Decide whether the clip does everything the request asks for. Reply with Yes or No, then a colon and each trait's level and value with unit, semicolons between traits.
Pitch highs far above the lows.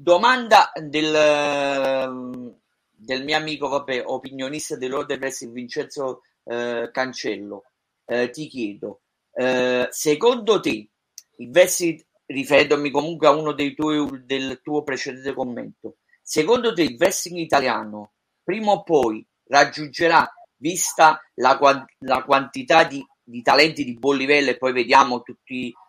No: average, 3.2 semitones